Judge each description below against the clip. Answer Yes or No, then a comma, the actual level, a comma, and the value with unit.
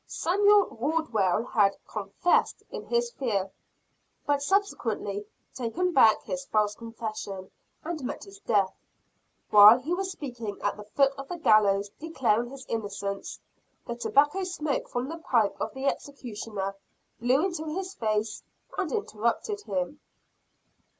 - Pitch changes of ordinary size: No, wide, 7.4 semitones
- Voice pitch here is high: Yes, high, 245 Hz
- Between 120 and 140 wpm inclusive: Yes, slow, 135 wpm